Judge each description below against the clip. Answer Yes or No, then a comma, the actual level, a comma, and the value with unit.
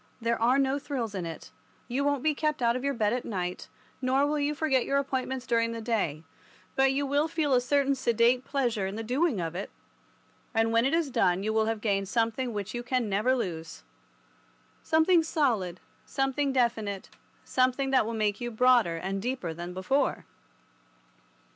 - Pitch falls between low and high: No, high, 240 Hz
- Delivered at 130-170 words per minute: No, average, 185 wpm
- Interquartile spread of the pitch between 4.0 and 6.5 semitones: Yes, average, 4.9 semitones